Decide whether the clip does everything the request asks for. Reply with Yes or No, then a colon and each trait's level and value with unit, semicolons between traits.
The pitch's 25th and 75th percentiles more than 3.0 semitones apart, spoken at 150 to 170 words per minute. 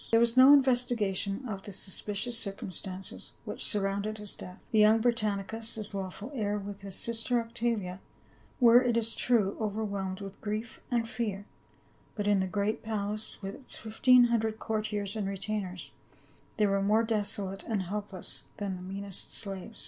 No: narrow, 2.5 semitones; average, 165 wpm